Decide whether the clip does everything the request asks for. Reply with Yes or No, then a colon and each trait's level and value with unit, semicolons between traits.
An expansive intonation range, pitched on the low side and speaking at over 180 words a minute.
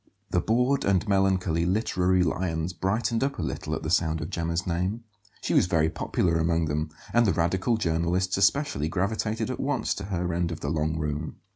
No: average, 4.0 semitones; very low, 90 Hz; average, 190 wpm